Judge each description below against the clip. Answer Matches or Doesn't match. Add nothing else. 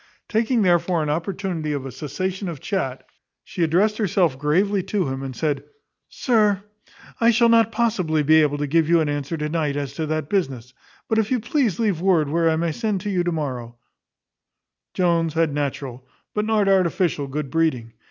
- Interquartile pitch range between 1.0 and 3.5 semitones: Doesn't match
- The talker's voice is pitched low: Doesn't match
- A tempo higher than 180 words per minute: Matches